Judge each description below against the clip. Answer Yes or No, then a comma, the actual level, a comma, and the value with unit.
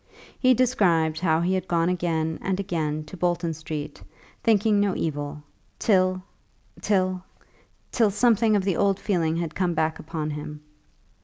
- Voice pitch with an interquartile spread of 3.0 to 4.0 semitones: Yes, average, 3.7 semitones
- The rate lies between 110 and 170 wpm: Yes, average, 150 wpm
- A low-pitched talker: No, medium, 175 Hz